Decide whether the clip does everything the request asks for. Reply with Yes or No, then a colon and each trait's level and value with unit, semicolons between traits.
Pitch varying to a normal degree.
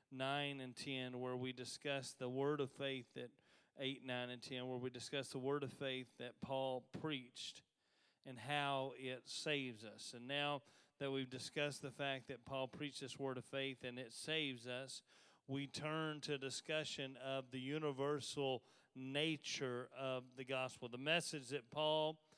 No: narrow, 2.1 semitones